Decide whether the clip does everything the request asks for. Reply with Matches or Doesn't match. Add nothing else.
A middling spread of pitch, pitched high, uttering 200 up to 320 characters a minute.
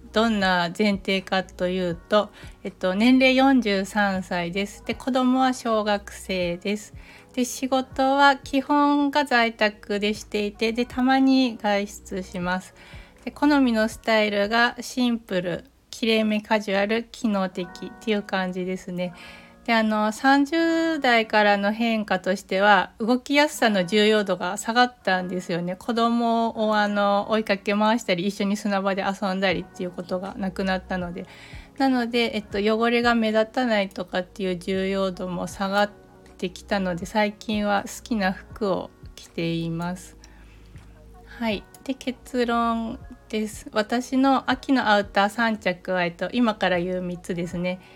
Matches